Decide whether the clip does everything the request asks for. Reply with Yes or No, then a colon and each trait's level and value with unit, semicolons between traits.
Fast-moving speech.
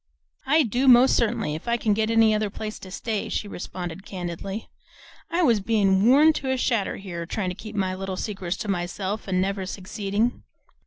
No: average, 195 wpm